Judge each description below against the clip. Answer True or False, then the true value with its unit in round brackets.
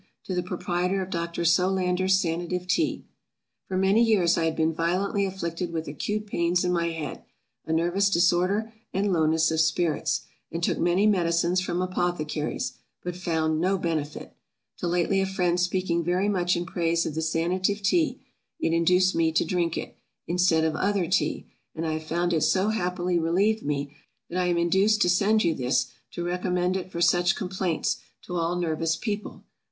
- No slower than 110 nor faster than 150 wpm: False (180 wpm)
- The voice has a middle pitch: True (175 Hz)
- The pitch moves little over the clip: True (2.1 semitones)